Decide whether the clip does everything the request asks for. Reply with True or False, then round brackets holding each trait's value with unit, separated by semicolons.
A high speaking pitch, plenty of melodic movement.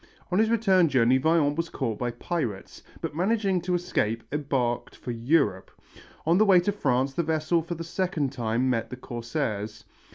False (150 Hz; 6.4 semitones)